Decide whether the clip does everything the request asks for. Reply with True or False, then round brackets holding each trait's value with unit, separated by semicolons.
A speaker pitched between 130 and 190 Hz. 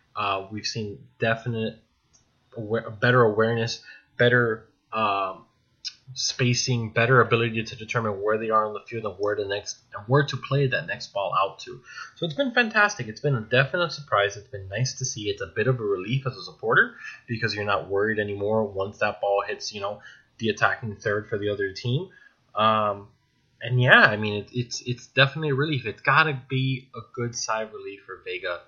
False (120 Hz)